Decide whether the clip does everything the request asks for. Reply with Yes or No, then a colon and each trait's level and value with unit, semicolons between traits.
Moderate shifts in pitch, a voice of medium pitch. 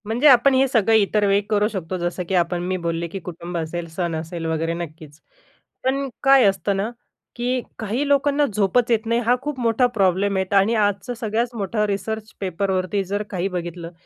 No: average, 4.8 semitones; high, 200 Hz